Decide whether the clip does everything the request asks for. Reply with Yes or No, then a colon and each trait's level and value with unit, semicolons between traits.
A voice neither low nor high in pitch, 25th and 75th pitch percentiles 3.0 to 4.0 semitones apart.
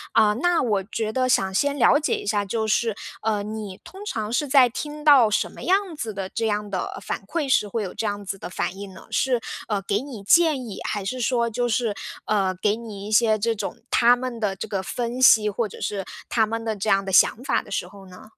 No: high, 220 Hz; average, 3.5 semitones